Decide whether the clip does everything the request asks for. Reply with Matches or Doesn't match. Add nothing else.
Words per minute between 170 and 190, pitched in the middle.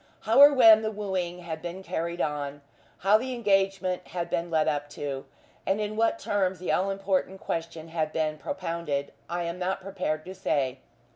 Matches